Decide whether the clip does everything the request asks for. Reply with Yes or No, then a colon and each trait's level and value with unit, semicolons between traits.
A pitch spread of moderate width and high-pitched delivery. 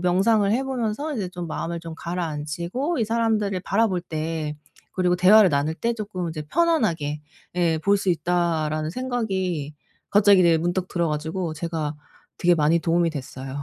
No: average, 4.3 semitones; medium, 175 Hz